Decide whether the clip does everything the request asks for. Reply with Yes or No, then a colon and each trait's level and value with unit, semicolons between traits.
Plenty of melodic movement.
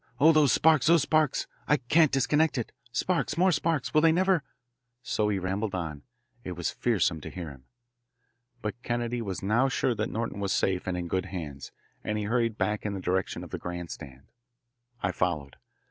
Yes: wide, 7.3 semitones